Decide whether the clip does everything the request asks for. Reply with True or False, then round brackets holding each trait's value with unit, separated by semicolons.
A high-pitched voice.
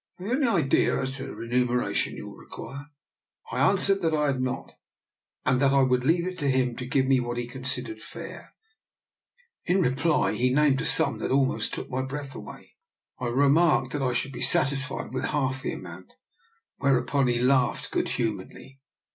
False (135 Hz)